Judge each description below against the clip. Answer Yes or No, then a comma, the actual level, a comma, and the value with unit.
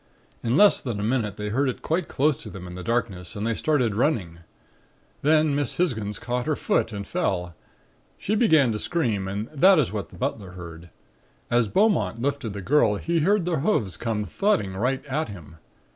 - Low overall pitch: Yes, low, 120 Hz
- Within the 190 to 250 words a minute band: Yes, average, 195 wpm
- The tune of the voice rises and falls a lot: Yes, wide, 7.0 semitones